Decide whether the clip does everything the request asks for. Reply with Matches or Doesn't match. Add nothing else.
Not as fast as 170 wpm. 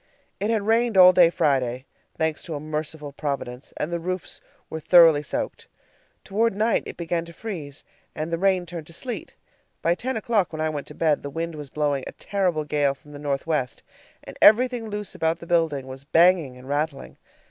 Doesn't match